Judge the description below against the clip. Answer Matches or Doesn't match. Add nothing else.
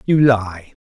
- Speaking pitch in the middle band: Doesn't match